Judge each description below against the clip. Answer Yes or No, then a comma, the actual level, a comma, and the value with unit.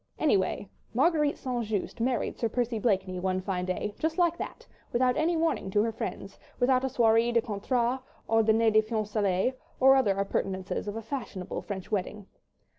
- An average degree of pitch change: Yes, average, 4.3 semitones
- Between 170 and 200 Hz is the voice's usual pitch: No, high, 225 Hz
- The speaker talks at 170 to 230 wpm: Yes, average, 175 wpm